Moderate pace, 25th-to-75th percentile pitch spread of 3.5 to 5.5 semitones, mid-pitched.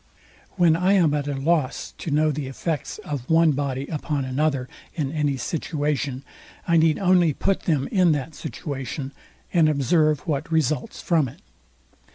No: average, 160 wpm; average, 2.9 semitones; medium, 150 Hz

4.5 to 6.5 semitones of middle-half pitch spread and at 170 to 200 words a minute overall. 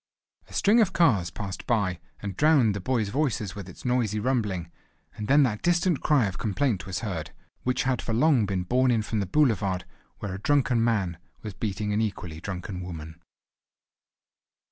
Yes: average, 5.2 semitones; average, 180 wpm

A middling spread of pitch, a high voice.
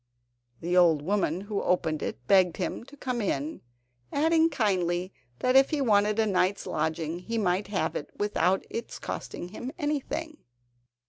No: wide, 5.7 semitones; high, 200 Hz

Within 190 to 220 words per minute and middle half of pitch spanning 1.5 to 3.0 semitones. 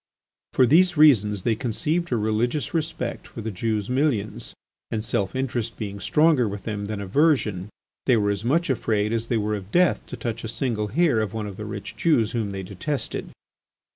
No: average, 195 wpm; average, 4.3 semitones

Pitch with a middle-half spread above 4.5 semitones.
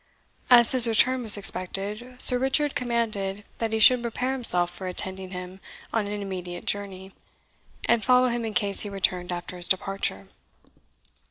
No: average, 4.1 semitones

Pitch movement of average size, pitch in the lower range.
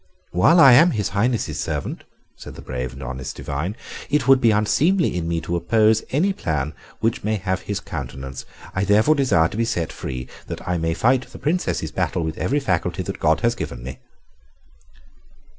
No: wide, 7.6 semitones; low, 100 Hz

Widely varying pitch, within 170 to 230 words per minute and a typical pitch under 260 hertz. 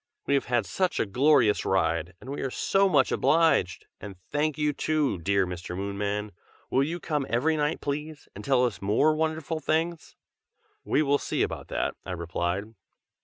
Yes: wide, 7.6 semitones; average, 175 wpm; low, 135 Hz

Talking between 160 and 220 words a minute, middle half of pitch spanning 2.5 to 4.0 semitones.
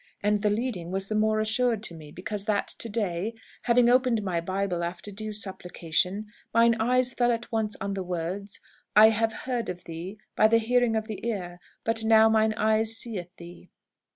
Yes: average, 190 wpm; average, 3.3 semitones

